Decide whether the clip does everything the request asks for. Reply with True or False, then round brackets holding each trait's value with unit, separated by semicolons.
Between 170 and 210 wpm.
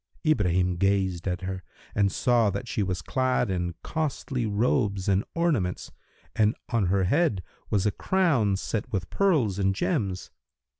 False (150 wpm)